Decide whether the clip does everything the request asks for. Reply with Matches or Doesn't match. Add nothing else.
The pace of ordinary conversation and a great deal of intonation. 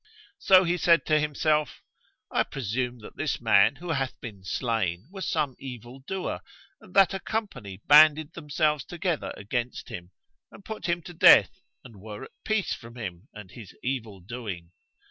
Matches